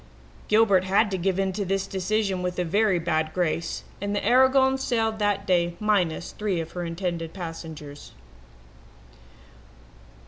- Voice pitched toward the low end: No, high, 190 Hz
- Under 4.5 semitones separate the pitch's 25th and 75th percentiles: Yes, average, 3.5 semitones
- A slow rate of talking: No, average, 145 wpm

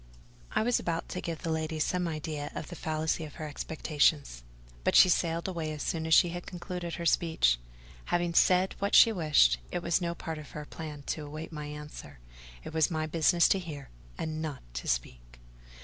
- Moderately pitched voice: Yes, medium, 160 Hz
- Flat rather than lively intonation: Yes, narrow, 2.3 semitones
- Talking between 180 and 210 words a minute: Yes, average, 200 wpm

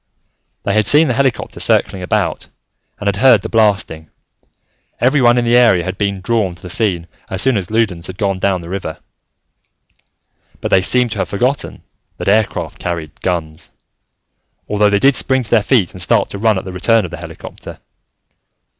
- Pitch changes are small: No, average, 4.2 semitones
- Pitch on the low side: Yes, low, 100 Hz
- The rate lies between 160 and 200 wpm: Yes, average, 185 wpm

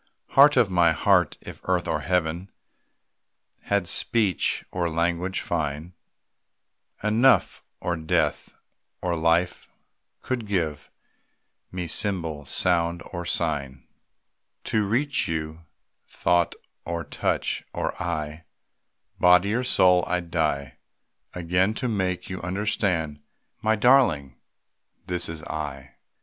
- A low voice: Yes, very low, 90 Hz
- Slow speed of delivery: Yes, slow, 110 wpm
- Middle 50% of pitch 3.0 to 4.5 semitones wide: Yes, average, 3.5 semitones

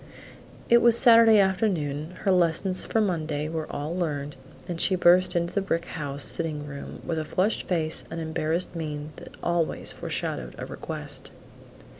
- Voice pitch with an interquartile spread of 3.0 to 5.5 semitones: Yes, average, 3.3 semitones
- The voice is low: No, medium, 170 Hz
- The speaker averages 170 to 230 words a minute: No, average, 160 wpm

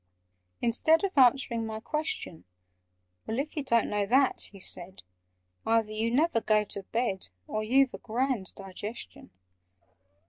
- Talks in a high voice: Yes, high, 230 Hz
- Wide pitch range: No, average, 4.2 semitones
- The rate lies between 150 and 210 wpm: No, average, 140 wpm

